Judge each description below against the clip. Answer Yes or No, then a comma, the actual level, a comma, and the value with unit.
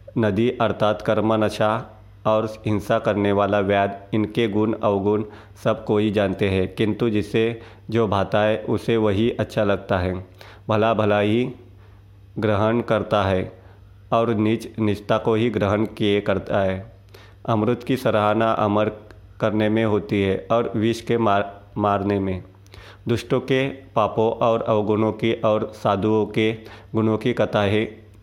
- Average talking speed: Yes, average, 140 wpm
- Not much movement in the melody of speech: Yes, narrow, 1.7 semitones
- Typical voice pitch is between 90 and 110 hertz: Yes, low, 105 Hz